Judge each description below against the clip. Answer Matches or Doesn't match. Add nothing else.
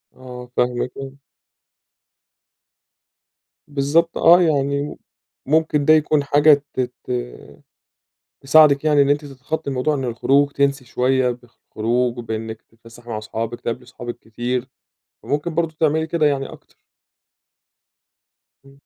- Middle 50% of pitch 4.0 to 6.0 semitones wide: Doesn't match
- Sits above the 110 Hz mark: Matches